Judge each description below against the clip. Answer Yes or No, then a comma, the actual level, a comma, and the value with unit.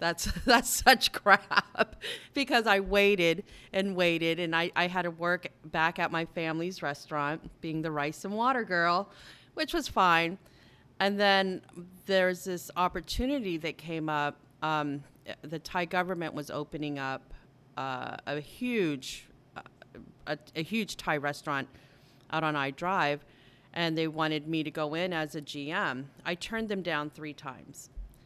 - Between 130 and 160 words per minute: Yes, average, 155 wpm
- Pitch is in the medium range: Yes, medium, 160 Hz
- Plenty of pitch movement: No, average, 3.8 semitones